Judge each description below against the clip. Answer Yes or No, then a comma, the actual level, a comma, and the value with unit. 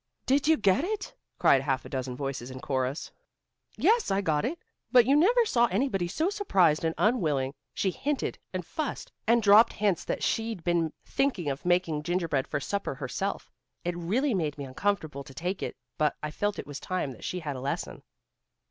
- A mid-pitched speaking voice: Yes, medium, 180 Hz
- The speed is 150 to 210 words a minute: Yes, average, 190 wpm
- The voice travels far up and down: Yes, wide, 7.9 semitones